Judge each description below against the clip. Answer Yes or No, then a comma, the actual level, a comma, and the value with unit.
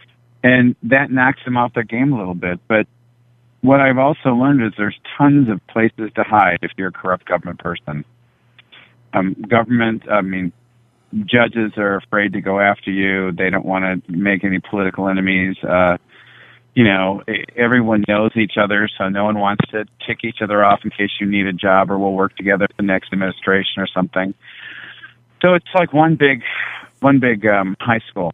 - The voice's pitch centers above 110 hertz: No, low, 105 Hz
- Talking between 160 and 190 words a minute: Yes, average, 185 wpm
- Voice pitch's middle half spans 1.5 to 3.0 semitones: No, average, 3.9 semitones